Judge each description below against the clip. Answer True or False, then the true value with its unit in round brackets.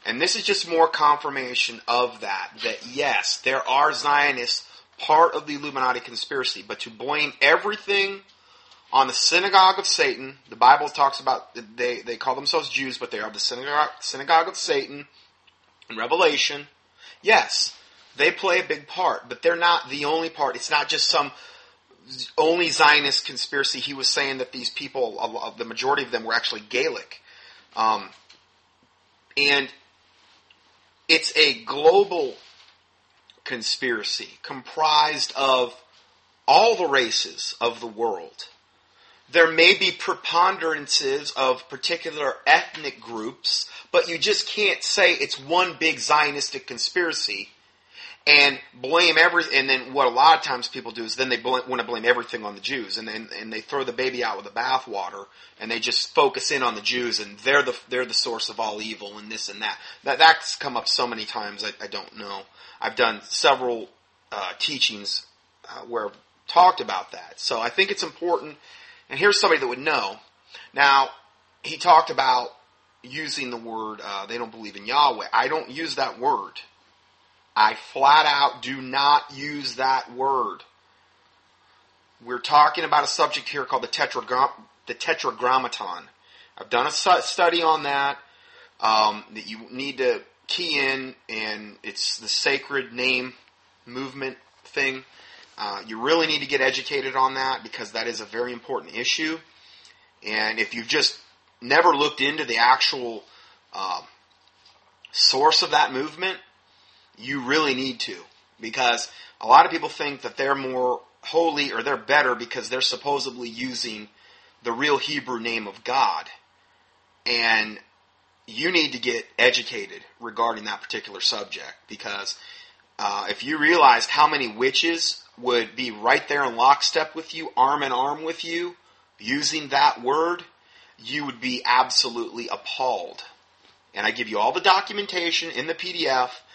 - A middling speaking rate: True (160 wpm)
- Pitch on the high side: False (140 Hz)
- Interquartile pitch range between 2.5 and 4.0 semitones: False (5.2 semitones)